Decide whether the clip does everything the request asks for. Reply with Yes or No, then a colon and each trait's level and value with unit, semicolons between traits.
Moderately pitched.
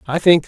Yes: medium, 160 Hz